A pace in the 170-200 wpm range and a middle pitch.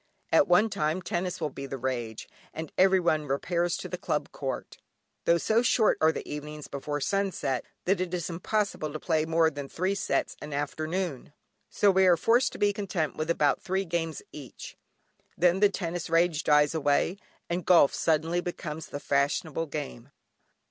Yes: average, 175 wpm; medium, 165 Hz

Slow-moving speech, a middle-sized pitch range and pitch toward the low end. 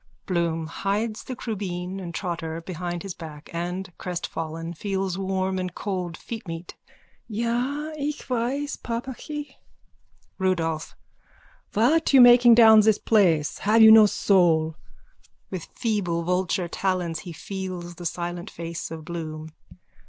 No: slow, 125 wpm; average, 4.6 semitones; medium, 185 Hz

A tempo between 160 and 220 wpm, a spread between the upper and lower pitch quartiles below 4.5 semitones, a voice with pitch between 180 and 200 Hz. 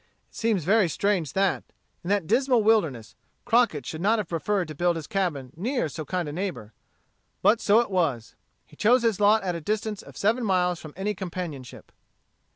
No: average, 190 wpm; average, 4.8 semitones; high, 190 Hz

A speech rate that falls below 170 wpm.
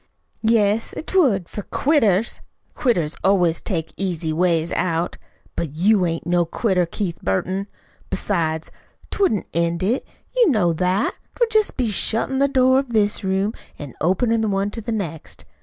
Yes: average, 155 wpm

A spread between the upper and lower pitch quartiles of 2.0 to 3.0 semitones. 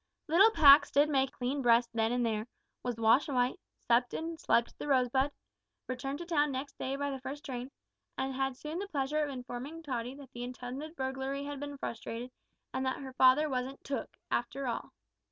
Yes: narrow, 2.6 semitones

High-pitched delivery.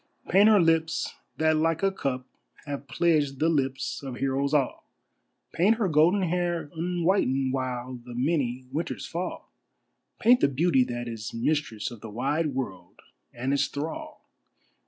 No: medium, 145 Hz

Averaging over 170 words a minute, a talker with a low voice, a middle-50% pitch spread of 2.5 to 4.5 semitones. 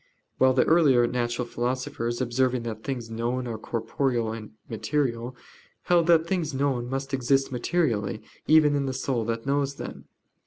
No: average, 155 wpm; low, 130 Hz; average, 2.9 semitones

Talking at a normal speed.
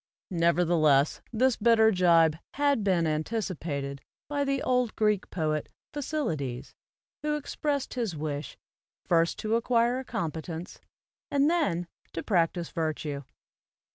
No: slow, 115 wpm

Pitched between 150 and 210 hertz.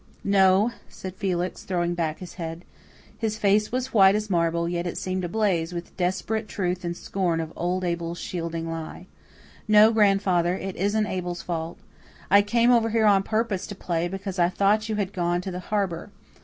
Yes: medium, 185 Hz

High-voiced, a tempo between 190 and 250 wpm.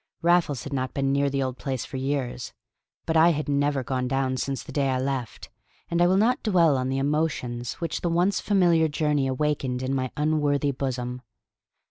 No: medium, 140 Hz; average, 195 wpm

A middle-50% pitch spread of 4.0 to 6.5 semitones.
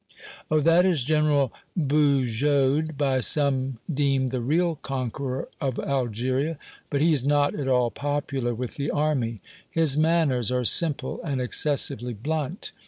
No: average, 3.0 semitones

